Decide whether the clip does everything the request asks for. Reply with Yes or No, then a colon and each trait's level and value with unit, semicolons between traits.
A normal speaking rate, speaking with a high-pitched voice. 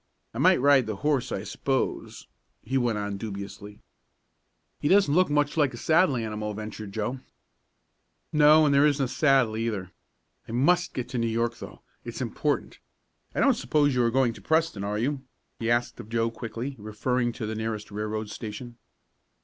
No: average, 180 wpm; low, 120 Hz